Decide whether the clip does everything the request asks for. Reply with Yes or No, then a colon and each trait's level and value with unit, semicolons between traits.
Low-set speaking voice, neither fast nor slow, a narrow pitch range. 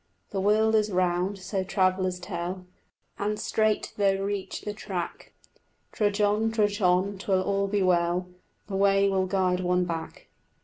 No: high, 195 Hz; average, 150 wpm; narrow, 2.0 semitones